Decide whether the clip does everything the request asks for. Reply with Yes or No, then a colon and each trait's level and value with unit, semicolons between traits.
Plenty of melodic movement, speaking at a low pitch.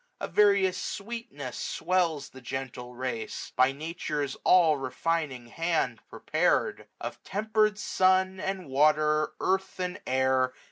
No: wide, 6.1 semitones; medium, 155 Hz